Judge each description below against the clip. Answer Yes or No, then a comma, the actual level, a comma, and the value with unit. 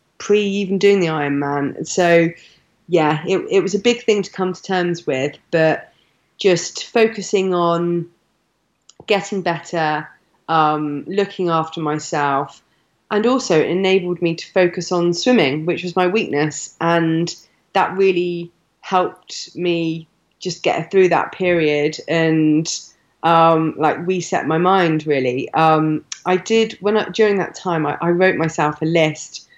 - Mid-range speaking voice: Yes, medium, 170 Hz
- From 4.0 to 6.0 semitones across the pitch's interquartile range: No, average, 3.0 semitones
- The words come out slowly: No, average, 150 wpm